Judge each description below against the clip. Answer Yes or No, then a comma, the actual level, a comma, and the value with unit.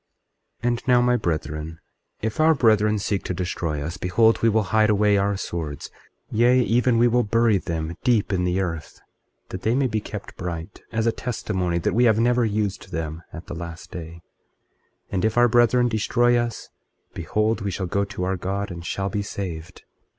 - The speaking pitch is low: Yes, low, 100 Hz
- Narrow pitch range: No, average, 4.6 semitones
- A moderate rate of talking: Yes, average, 195 wpm